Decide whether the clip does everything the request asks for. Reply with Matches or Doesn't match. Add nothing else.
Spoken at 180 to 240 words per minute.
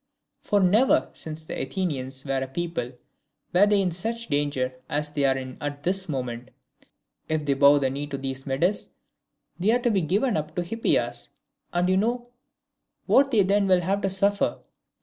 Matches